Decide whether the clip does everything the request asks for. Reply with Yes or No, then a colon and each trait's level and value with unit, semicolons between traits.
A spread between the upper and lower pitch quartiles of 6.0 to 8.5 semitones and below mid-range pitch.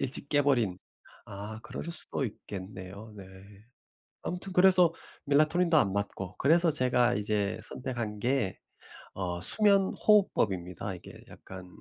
Yes: wide, 8.0 semitones; low, 120 Hz